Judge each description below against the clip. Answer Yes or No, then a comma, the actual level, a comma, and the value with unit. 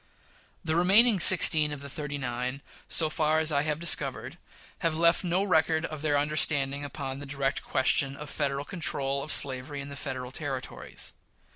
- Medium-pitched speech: Yes, medium, 145 Hz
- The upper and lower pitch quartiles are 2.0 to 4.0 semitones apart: Yes, narrow, 2.5 semitones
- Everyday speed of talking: Yes, average, 170 wpm